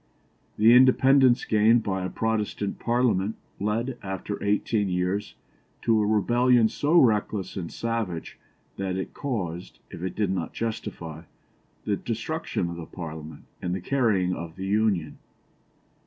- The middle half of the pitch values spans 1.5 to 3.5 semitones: No, average, 4.0 semitones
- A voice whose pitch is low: Yes, low, 105 Hz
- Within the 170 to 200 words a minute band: No, average, 140 wpm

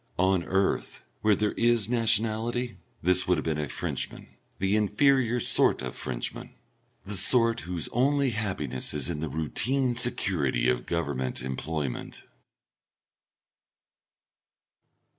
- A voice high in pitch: No, very low, 95 Hz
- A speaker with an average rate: No, slow, 120 wpm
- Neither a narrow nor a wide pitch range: No, wide, 7.2 semitones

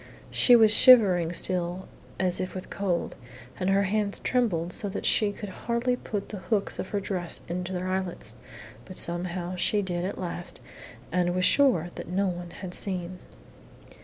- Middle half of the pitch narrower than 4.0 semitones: Yes, narrow, 2.4 semitones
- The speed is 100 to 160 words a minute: No, average, 170 wpm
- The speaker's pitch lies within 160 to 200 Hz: Yes, medium, 185 Hz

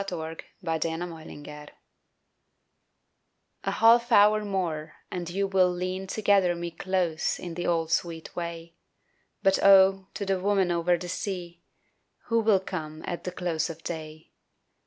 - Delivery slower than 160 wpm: Yes, average, 150 wpm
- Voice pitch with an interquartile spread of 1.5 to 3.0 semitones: Yes, average, 2.7 semitones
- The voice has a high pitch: No, medium, 180 Hz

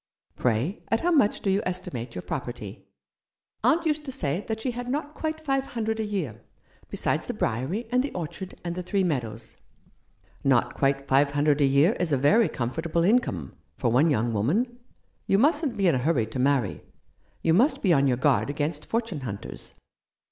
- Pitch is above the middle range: No, medium, 165 Hz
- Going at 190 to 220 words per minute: Yes, fast, 205 wpm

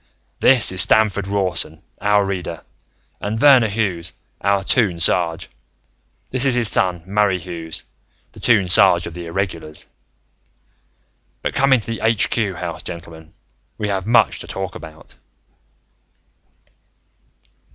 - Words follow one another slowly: Yes, slow, 130 wpm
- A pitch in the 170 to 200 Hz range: No, very low, 95 Hz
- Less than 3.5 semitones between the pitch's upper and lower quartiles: No, average, 3.8 semitones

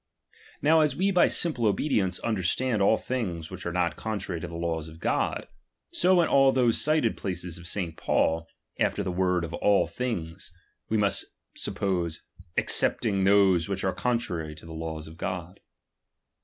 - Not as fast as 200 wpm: Yes, average, 160 wpm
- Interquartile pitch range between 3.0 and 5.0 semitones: No, wide, 5.5 semitones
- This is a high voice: No, very low, 95 Hz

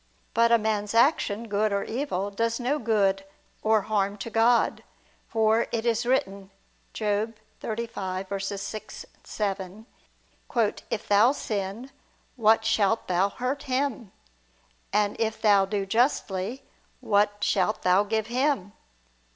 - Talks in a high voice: Yes, high, 215 Hz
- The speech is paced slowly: Yes, slow, 120 wpm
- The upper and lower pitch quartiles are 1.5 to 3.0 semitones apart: Yes, narrow, 2.6 semitones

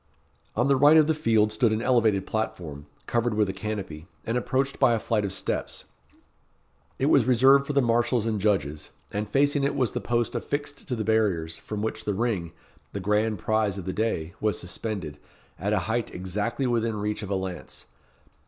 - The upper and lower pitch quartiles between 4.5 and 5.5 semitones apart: No, average, 3.4 semitones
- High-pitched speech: No, low, 110 Hz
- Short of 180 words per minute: No, average, 195 wpm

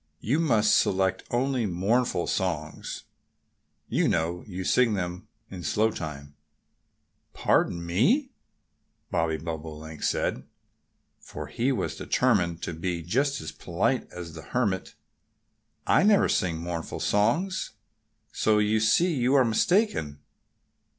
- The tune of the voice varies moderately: No, wide, 6.8 semitones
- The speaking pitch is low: Yes, very low, 95 Hz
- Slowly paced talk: Yes, slow, 120 wpm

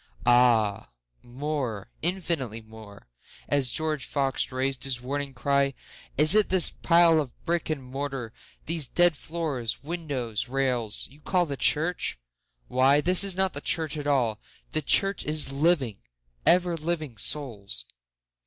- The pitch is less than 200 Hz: Yes, medium, 140 Hz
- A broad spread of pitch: No, average, 4.8 semitones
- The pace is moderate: No, slow, 120 wpm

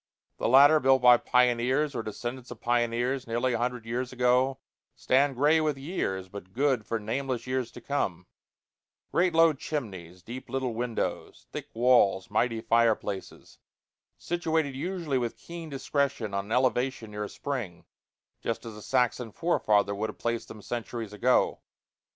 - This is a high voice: No, low, 125 Hz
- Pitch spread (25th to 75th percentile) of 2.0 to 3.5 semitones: Yes, average, 3.1 semitones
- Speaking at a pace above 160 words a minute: No, average, 155 wpm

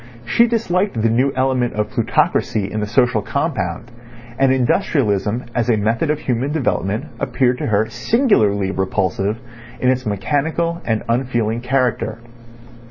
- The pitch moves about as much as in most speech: Yes, average, 4.3 semitones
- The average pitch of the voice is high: No, low, 120 Hz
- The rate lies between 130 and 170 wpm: Yes, average, 140 wpm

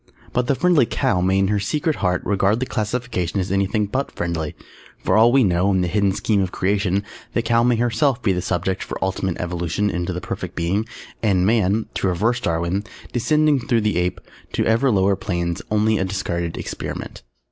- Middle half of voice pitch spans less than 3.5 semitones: No, average, 4.2 semitones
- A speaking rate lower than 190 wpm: No, average, 200 wpm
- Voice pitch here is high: No, low, 100 Hz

